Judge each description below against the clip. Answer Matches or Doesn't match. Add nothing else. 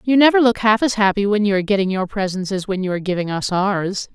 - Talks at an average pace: Doesn't match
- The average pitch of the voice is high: Matches